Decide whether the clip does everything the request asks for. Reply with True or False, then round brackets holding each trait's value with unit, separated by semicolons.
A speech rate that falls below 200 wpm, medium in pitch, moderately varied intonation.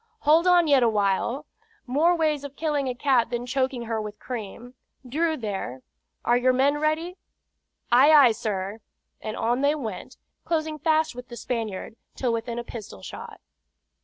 False (160 wpm; 250 Hz; 4.8 semitones)